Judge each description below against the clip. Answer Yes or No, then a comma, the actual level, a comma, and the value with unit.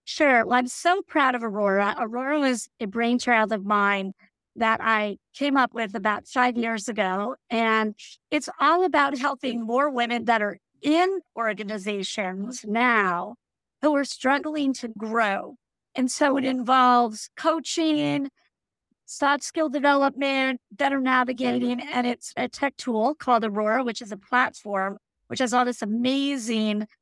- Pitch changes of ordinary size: Yes, average, 4.0 semitones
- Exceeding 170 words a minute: No, average, 145 wpm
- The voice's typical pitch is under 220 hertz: No, high, 245 Hz